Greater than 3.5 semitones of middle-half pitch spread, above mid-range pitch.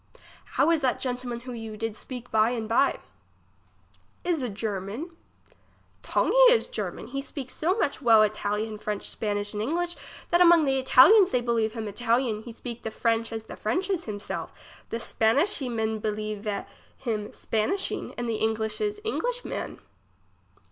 Yes: average, 4.6 semitones; high, 235 Hz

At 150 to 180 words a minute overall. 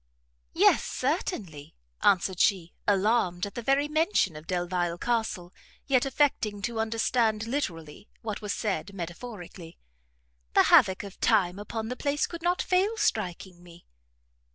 No: slow, 135 wpm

